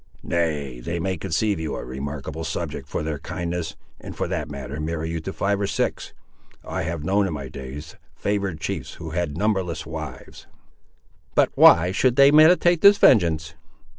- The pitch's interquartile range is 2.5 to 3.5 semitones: No, average, 4.1 semitones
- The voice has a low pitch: Yes, very low, 80 Hz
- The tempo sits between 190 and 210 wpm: No, average, 170 wpm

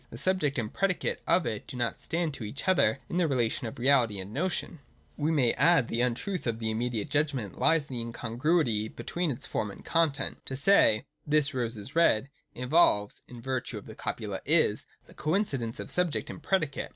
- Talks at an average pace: No, fast, 210 wpm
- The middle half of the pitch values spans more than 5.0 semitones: Yes, wide, 5.6 semitones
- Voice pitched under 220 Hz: Yes, low, 135 Hz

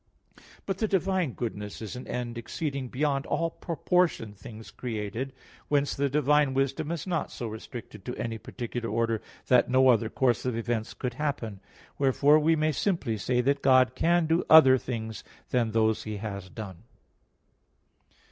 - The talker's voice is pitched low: Yes, low, 125 Hz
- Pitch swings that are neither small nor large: Yes, average, 4.7 semitones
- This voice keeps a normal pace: Yes, average, 160 wpm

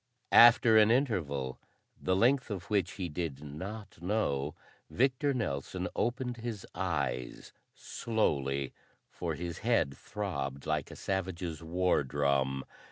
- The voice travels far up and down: Yes, wide, 7.7 semitones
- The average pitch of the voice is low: Yes, very low, 90 Hz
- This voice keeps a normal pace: No, slow, 120 wpm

